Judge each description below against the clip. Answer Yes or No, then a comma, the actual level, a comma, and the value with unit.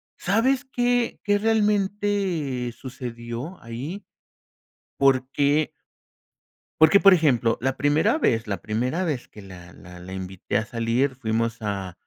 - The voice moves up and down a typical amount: No, wide, 8.9 semitones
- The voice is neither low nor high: No, low, 130 Hz